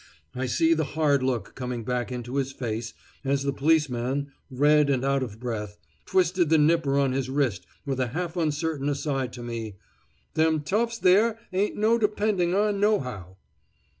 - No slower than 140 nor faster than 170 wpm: Yes, average, 165 wpm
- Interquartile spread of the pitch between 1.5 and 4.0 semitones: No, average, 4.7 semitones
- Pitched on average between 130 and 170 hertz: Yes, medium, 140 Hz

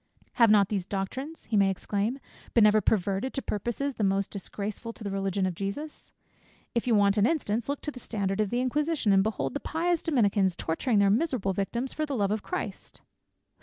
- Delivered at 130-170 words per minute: No, fast, 205 wpm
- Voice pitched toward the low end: No, high, 210 Hz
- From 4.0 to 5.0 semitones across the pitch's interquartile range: Yes, average, 4.5 semitones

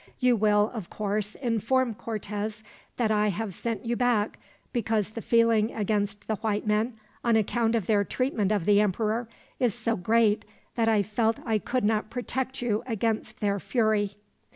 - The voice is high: Yes, high, 220 Hz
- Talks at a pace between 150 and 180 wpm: Yes, average, 175 wpm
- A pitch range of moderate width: No, narrow, 1.9 semitones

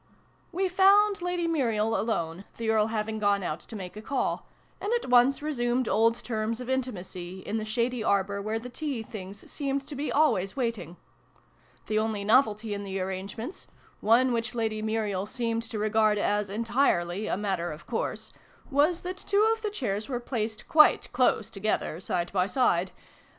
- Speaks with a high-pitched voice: Yes, high, 220 Hz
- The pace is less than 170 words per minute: No, average, 175 wpm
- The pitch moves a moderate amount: Yes, average, 4.3 semitones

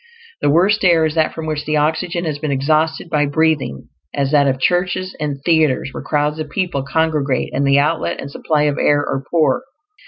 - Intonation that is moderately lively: No, narrow, 2.2 semitones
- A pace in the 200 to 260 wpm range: Yes, fast, 205 wpm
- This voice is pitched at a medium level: Yes, medium, 150 Hz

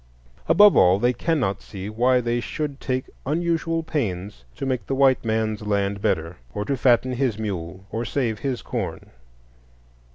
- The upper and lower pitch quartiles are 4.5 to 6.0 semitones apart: Yes, average, 5.1 semitones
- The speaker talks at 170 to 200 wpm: No, average, 160 wpm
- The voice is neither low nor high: No, low, 120 Hz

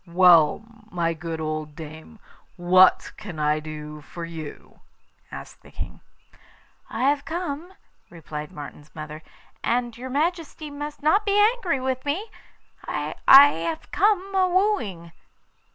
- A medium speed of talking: No, slow, 130 wpm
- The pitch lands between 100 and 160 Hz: No, high, 190 Hz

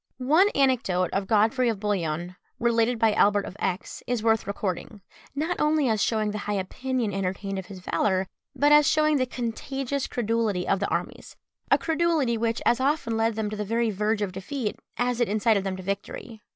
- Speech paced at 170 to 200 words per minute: Yes, average, 190 wpm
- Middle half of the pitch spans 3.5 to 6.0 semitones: Yes, average, 4.1 semitones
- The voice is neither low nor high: No, high, 225 Hz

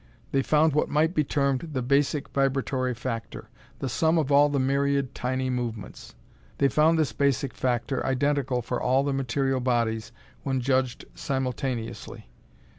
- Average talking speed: Yes, average, 150 wpm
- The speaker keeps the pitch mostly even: Yes, narrow, 2.0 semitones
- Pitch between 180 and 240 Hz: No, low, 135 Hz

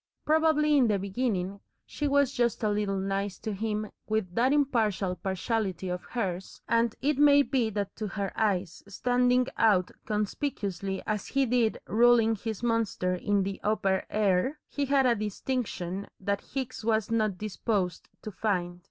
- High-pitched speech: Yes, high, 215 Hz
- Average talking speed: Yes, average, 160 wpm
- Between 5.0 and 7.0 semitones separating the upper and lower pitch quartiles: No, average, 4.0 semitones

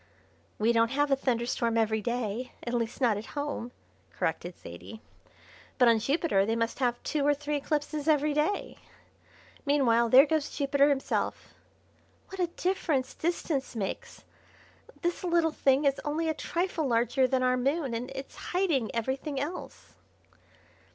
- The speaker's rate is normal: Yes, average, 150 wpm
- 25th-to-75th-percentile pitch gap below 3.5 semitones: No, average, 4.3 semitones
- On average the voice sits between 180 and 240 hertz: No, very high, 270 Hz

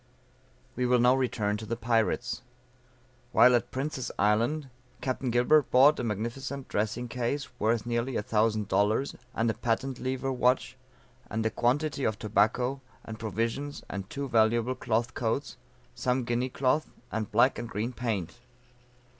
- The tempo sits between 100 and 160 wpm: Yes, average, 150 wpm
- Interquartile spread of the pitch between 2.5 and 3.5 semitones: Yes, average, 2.8 semitones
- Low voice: Yes, low, 120 Hz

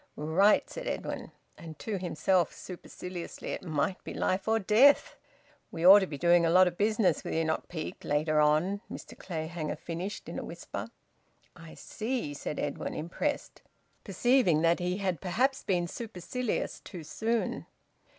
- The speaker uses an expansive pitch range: No, average, 4.4 semitones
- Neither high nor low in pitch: Yes, medium, 180 Hz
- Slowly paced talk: No, average, 155 wpm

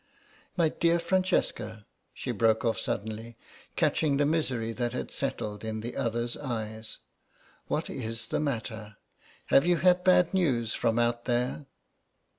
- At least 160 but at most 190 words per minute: No, average, 140 wpm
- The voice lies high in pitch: No, low, 120 Hz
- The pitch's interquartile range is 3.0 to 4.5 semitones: No, average, 5.1 semitones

